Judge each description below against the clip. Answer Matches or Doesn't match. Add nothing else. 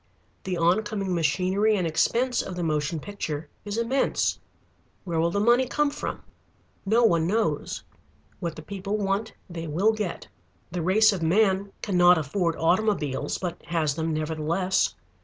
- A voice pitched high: Doesn't match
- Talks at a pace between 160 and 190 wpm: Doesn't match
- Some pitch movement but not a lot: Matches